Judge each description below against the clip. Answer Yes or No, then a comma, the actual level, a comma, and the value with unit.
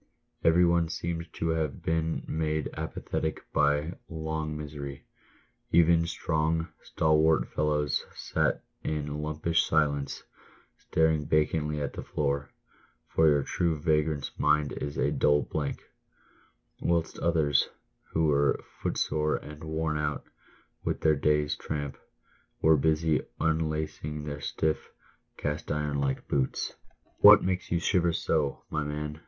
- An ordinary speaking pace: No, slow, 125 wpm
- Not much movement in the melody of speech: Yes, narrow, 1.5 semitones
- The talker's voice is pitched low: Yes, very low, 75 Hz